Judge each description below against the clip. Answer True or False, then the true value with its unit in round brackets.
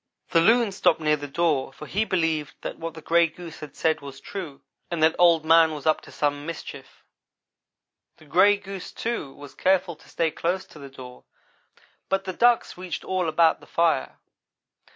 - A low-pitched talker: False (165 Hz)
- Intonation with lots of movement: False (3.4 semitones)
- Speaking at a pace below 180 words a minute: False (190 wpm)